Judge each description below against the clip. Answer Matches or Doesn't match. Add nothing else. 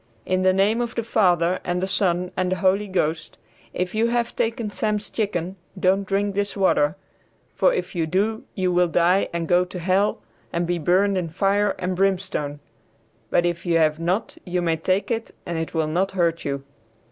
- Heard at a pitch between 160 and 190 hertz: Matches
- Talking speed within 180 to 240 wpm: Matches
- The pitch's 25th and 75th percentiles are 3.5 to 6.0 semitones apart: Doesn't match